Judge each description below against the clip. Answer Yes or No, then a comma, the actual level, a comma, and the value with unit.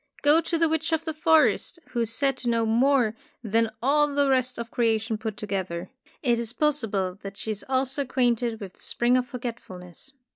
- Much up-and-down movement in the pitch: No, average, 4.0 semitones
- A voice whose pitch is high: Yes, high, 240 Hz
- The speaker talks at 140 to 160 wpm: No, fast, 205 wpm